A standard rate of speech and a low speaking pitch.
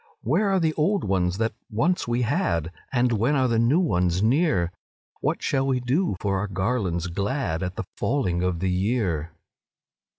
Yes: average, 175 wpm; low, 110 Hz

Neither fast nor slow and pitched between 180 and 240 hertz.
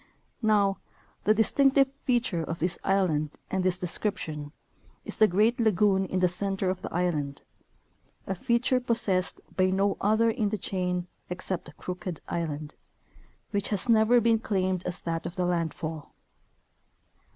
Yes: average, 145 wpm; high, 190 Hz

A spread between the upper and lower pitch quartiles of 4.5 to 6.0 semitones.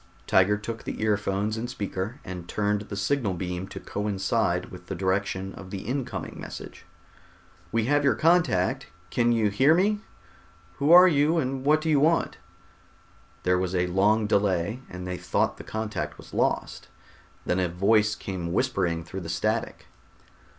Yes: average, 5.0 semitones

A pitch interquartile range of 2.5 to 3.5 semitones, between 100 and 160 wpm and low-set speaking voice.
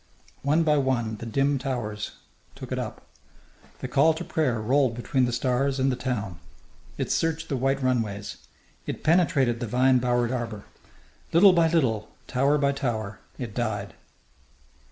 Yes: average, 3.2 semitones; average, 155 wpm; low, 130 Hz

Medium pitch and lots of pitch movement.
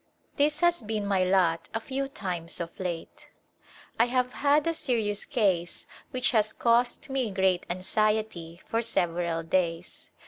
No: high, 210 Hz; wide, 6.0 semitones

